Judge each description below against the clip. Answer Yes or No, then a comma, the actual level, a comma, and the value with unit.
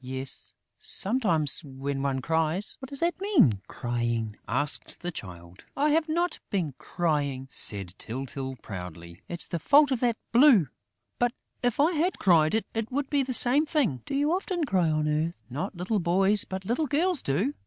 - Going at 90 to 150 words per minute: No, average, 175 wpm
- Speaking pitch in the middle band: Yes, medium, 180 Hz